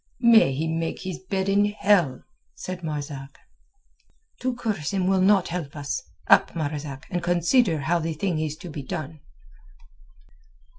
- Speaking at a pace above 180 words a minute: No, average, 150 wpm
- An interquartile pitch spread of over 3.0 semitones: Yes, average, 4.2 semitones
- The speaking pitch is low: No, medium, 170 Hz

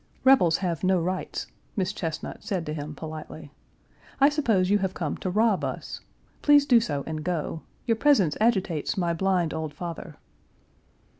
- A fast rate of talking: No, average, 160 wpm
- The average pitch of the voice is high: No, medium, 180 Hz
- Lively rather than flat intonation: No, average, 4.9 semitones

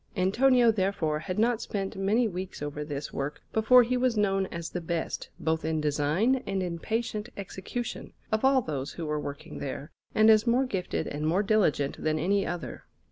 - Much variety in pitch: Yes, wide, 6.0 semitones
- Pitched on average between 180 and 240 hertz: Yes, high, 190 Hz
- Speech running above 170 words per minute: Yes, average, 190 wpm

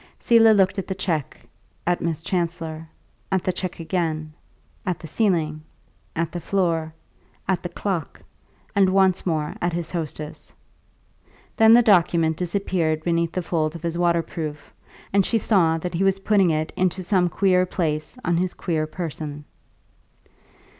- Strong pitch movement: No, average, 2.8 semitones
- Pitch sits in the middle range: Yes, medium, 175 Hz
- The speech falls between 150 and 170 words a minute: Yes, average, 155 wpm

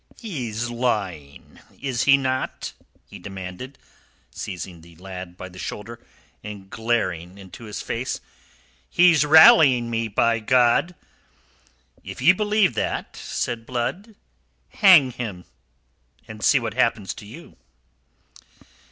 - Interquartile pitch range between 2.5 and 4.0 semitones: No, average, 5.2 semitones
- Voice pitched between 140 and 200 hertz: No, low, 115 Hz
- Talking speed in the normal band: No, slow, 115 wpm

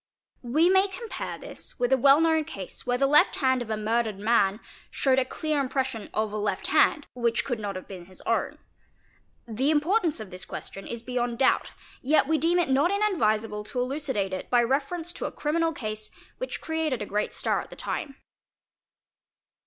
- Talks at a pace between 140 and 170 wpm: No, average, 190 wpm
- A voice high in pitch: Yes, very high, 255 Hz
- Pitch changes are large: Yes, wide, 6.1 semitones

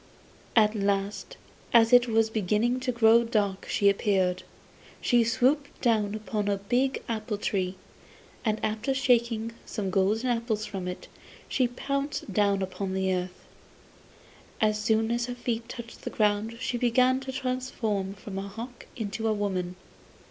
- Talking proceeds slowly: No, average, 150 wpm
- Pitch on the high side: Yes, high, 220 Hz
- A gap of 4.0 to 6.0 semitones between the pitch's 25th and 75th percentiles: No, average, 3.2 semitones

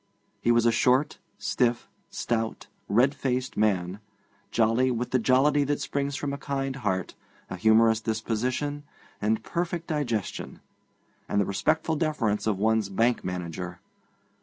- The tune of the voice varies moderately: Yes, average, 4.4 semitones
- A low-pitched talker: Yes, low, 120 Hz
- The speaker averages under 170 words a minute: Yes, slow, 135 wpm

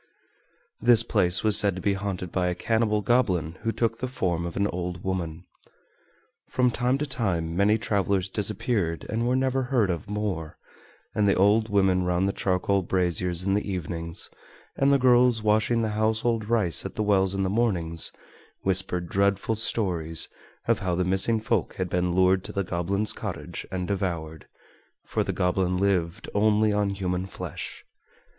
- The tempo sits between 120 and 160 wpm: No, average, 170 wpm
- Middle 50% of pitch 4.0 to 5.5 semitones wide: No, average, 3.3 semitones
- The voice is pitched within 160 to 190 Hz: No, low, 100 Hz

